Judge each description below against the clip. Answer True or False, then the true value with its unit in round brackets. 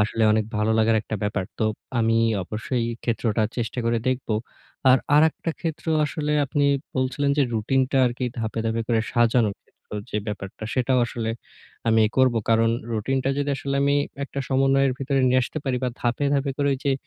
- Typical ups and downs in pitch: True (3.3 semitones)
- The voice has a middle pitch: False (125 Hz)